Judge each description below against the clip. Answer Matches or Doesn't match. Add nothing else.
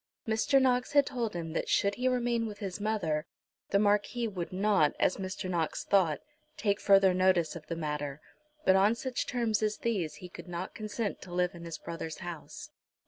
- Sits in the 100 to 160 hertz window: Doesn't match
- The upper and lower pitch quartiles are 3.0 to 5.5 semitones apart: Matches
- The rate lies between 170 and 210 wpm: Matches